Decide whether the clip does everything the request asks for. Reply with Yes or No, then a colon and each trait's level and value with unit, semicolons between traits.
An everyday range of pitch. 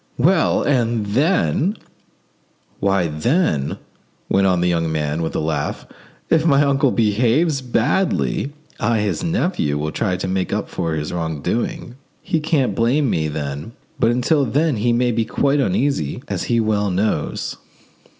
No: wide, 8.3 semitones